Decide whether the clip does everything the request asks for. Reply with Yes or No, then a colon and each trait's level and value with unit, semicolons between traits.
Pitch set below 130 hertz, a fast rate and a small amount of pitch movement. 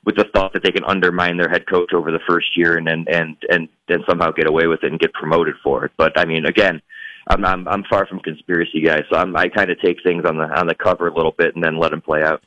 Yes: very low, 85 Hz; fast, 300 wpm; narrow, 2.0 semitones